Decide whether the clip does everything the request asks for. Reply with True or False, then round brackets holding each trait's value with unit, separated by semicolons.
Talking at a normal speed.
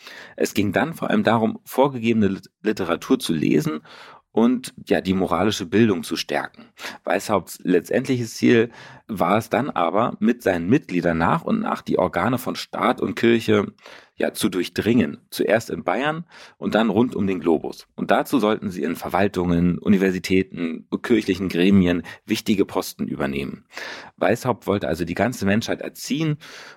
True (150 wpm)